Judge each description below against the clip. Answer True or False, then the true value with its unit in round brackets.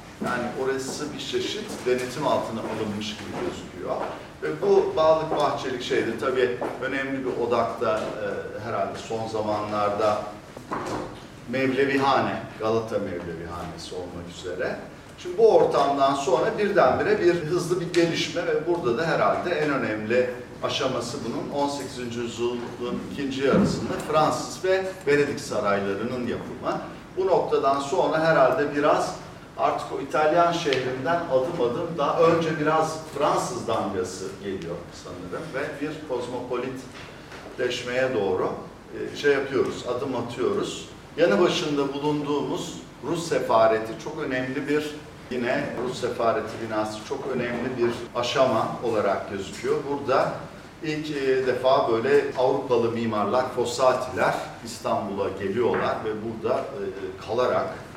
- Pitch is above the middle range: False (130 Hz)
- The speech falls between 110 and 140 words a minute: True (115 wpm)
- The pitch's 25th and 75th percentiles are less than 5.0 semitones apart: False (5.6 semitones)